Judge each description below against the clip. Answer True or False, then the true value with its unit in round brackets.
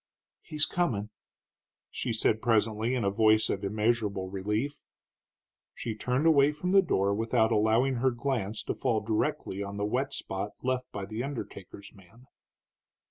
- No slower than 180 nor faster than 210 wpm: False (145 wpm)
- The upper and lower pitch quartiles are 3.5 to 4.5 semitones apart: True (3.9 semitones)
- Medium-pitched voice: False (110 Hz)